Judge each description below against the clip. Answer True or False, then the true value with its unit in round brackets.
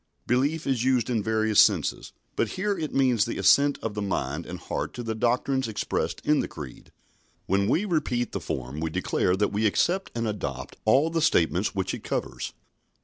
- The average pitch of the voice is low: True (115 Hz)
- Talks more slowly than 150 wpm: False (195 wpm)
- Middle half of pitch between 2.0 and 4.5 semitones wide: False (5.5 semitones)